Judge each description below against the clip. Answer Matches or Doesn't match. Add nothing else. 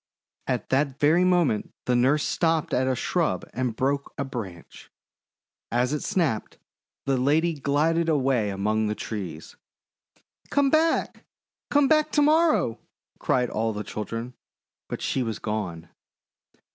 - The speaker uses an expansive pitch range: Matches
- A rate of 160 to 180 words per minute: Doesn't match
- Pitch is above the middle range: Doesn't match